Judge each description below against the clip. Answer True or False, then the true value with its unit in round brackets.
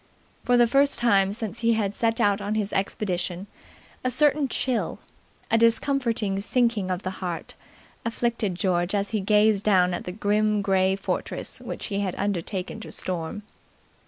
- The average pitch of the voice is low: False (205 Hz)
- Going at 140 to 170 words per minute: True (160 wpm)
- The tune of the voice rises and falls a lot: False (3.3 semitones)